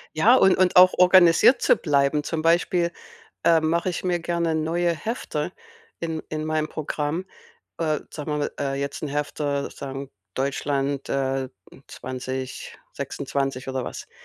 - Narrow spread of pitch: No, average, 3.6 semitones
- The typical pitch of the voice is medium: Yes, medium, 155 Hz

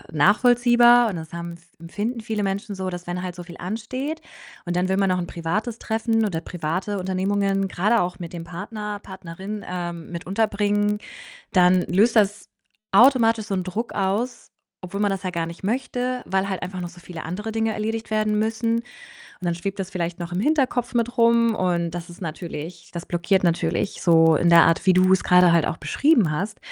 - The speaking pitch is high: Yes, high, 195 Hz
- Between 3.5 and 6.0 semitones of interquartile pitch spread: Yes, average, 4.0 semitones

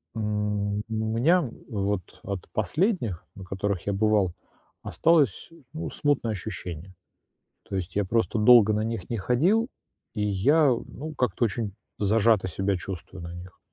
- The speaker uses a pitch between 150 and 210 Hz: No, low, 105 Hz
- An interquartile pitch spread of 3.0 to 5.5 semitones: Yes, average, 3.6 semitones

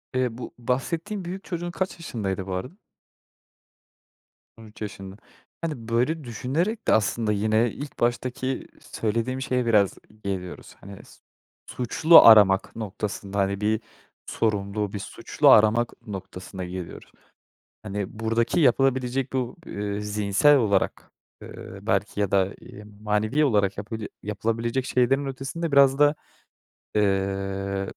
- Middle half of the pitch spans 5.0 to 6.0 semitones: No, average, 4.5 semitones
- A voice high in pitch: No, low, 110 Hz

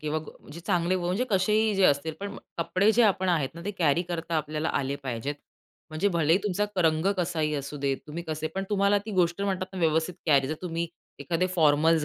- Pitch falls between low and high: Yes, medium, 170 Hz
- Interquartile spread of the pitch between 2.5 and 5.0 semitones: Yes, average, 3.5 semitones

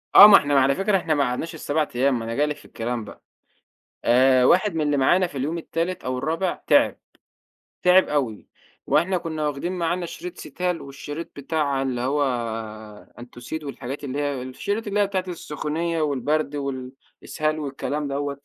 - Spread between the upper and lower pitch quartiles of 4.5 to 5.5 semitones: No, average, 3.7 semitones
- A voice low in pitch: No, medium, 145 Hz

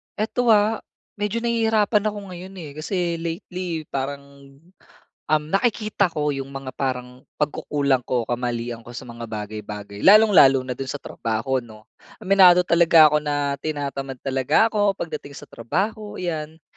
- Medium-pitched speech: Yes, medium, 150 Hz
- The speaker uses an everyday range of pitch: No, wide, 6.8 semitones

